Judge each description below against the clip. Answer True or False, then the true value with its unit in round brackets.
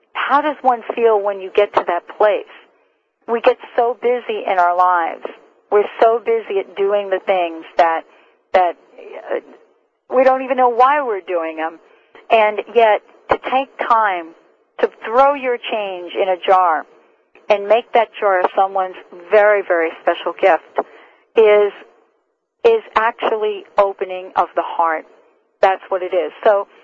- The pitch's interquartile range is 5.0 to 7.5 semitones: True (5.6 semitones)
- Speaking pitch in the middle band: False (215 Hz)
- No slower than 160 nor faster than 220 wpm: False (150 wpm)